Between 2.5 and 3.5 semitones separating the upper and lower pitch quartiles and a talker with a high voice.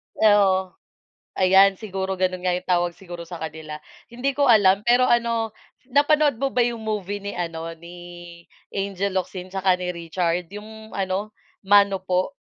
Yes: average, 3.2 semitones; high, 195 Hz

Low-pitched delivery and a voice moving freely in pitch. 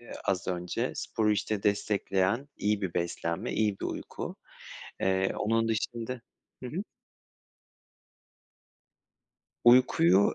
No: low, 105 Hz; average, 3.2 semitones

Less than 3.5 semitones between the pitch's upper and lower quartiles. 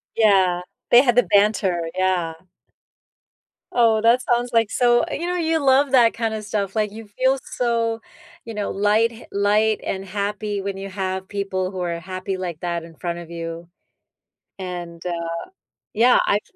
No: average, 3.8 semitones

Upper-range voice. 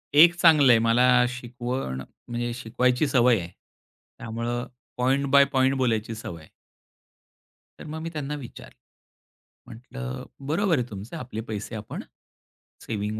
No: low, 120 Hz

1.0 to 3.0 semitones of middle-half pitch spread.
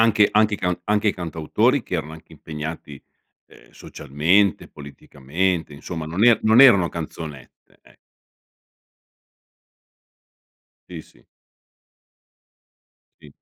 No: average, 5.2 semitones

